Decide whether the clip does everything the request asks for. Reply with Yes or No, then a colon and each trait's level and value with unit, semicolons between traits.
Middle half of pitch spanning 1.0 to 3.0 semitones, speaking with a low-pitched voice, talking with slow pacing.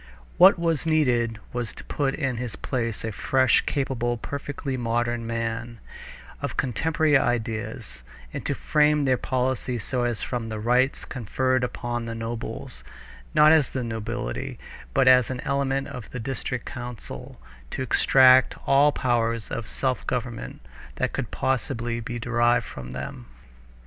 No: narrow, 2.4 semitones; low, 125 Hz; average, 150 wpm